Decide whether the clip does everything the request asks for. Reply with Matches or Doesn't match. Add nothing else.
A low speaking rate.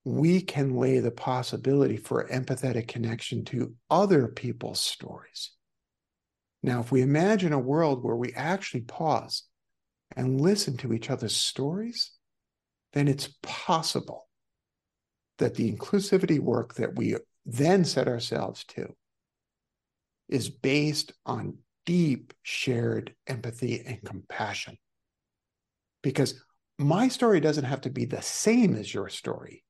Matches